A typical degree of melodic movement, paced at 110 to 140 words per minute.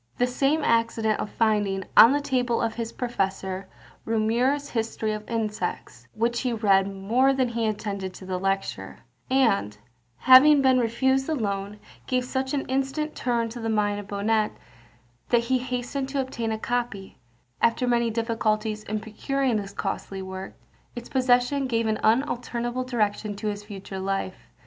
No: average, 3.3 semitones; average, 160 wpm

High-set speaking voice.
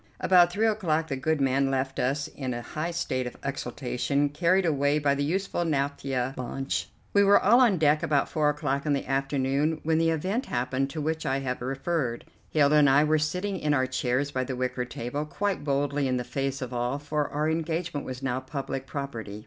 No: medium, 140 Hz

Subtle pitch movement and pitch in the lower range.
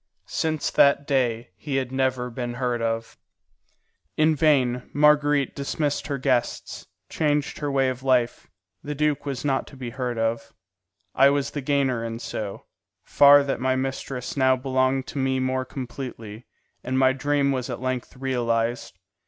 Yes: narrow, 2.2 semitones; low, 130 Hz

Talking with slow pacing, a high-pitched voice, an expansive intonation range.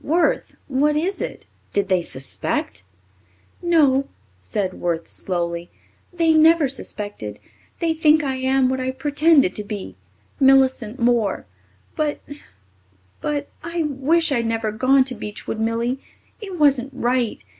Yes: slow, 130 wpm; very high, 260 Hz; wide, 5.8 semitones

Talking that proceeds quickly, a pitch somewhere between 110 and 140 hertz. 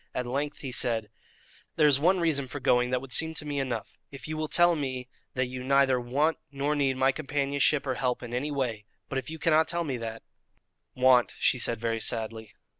Yes: fast, 220 wpm; low, 135 Hz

